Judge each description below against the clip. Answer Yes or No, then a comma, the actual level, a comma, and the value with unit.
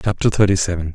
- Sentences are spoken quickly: No, average, 190 wpm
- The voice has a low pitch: Yes, very low, 90 Hz